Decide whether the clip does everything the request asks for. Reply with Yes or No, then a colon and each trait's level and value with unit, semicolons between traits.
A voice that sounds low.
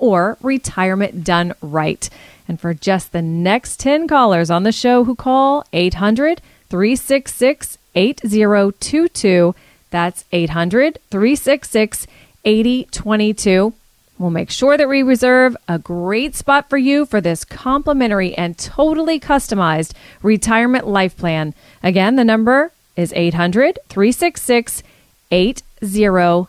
No: high, 215 Hz